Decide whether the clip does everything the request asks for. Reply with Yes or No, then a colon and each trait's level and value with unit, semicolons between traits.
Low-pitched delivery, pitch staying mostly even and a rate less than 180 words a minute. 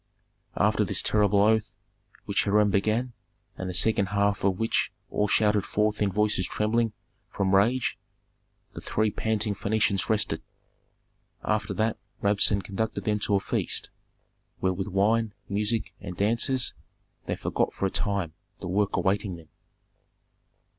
Yes: low, 105 Hz; narrow, 1.7 semitones; average, 140 wpm